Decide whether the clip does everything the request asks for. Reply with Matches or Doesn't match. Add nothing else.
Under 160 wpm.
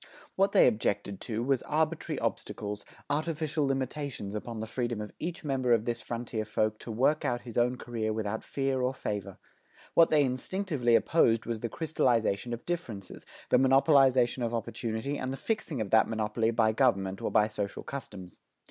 Doesn't match